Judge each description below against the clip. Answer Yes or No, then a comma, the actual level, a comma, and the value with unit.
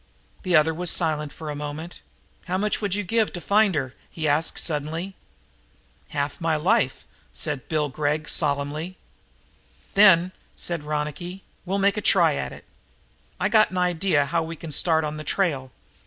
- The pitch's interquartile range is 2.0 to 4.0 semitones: Yes, average, 3.6 semitones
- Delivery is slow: No, average, 170 wpm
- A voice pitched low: No, medium, 160 Hz